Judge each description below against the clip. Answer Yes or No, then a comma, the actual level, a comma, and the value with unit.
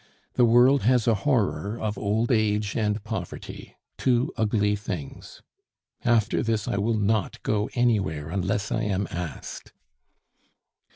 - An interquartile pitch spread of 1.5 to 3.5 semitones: Yes, narrow, 2.5 semitones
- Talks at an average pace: No, slow, 130 wpm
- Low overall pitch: Yes, low, 105 Hz